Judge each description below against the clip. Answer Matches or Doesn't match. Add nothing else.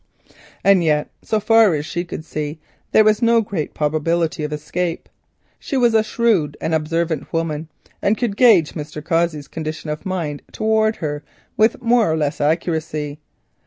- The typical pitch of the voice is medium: Matches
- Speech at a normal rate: Matches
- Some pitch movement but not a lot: Doesn't match